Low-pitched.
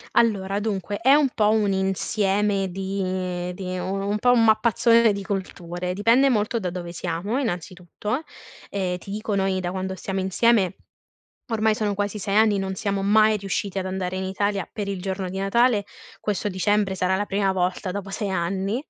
No: high, 195 Hz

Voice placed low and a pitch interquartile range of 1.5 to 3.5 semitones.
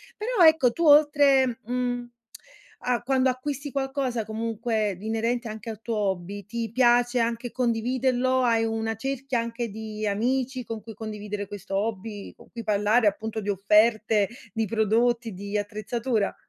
No: high, 230 Hz; average, 2.7 semitones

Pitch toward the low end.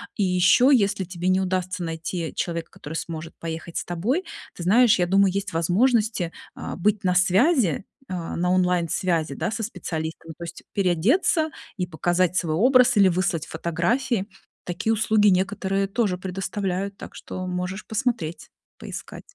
No: medium, 185 Hz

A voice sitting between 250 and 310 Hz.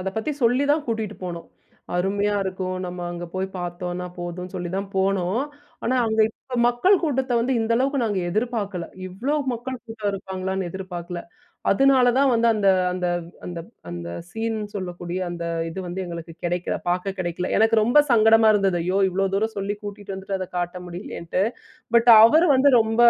No: high, 195 Hz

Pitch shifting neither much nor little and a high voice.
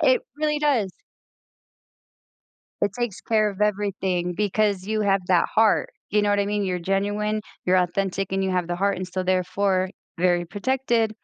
No: narrow, 2.3 semitones; high, 200 Hz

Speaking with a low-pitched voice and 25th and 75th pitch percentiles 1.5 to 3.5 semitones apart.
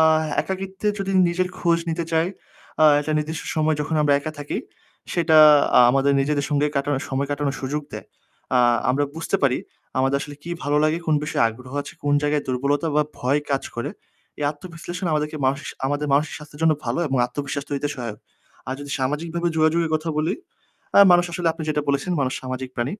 No: medium, 150 Hz; average, 2.7 semitones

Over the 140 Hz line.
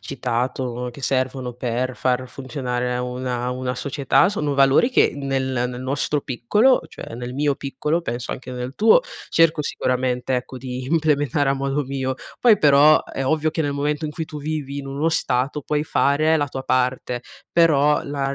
No: low, 135 Hz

